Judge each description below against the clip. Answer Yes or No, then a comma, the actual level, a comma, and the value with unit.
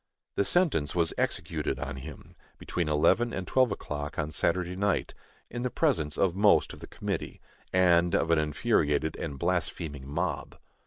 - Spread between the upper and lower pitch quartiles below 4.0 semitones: No, average, 4.6 semitones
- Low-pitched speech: Yes, very low, 85 Hz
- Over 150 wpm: Yes, average, 160 wpm